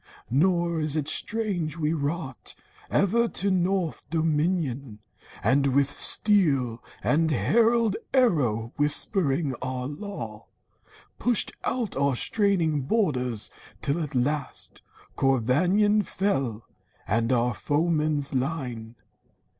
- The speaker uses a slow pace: Yes, slow, 105 wpm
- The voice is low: No, medium, 150 Hz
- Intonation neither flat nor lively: No, wide, 6.1 semitones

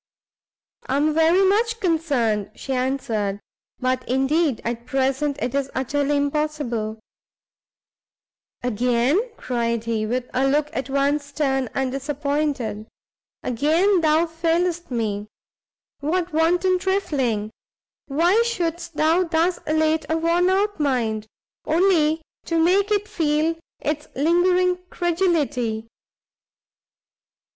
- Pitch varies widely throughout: No, average, 5.0 semitones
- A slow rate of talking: Yes, slow, 110 wpm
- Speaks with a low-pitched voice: No, very high, 300 Hz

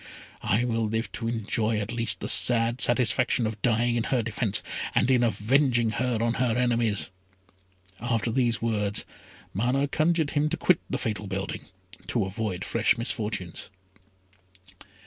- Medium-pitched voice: No, low, 115 Hz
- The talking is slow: No, average, 145 wpm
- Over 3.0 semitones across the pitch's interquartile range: No, narrow, 2.4 semitones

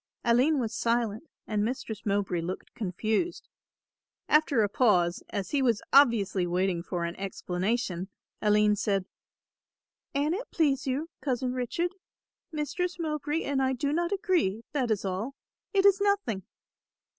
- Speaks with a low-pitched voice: No, high, 235 Hz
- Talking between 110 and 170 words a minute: Yes, average, 140 wpm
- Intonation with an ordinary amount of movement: No, wide, 6.9 semitones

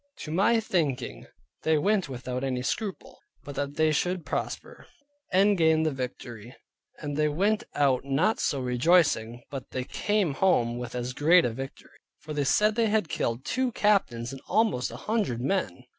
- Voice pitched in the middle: Yes, medium, 145 Hz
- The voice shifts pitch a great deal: Yes, wide, 7.1 semitones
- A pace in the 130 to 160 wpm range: No, average, 175 wpm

